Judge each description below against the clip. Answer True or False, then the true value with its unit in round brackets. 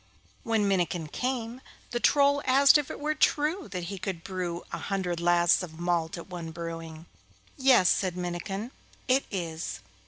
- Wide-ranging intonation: True (6.8 semitones)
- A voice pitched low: False (185 Hz)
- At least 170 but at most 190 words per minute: False (160 wpm)